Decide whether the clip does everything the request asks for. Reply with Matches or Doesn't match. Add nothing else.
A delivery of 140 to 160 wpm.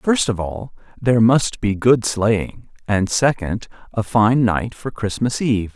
Matches